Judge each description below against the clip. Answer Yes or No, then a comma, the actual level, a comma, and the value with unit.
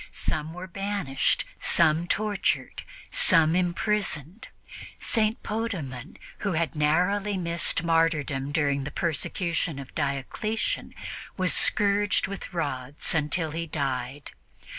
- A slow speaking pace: Yes, slow, 105 wpm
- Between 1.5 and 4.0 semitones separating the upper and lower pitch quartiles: No, average, 4.9 semitones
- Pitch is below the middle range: No, medium, 165 Hz